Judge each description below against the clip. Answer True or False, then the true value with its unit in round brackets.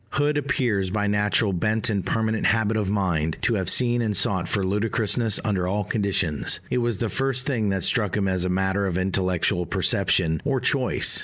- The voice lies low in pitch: True (105 Hz)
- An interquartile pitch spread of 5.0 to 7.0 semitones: False (3.4 semitones)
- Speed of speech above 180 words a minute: True (190 wpm)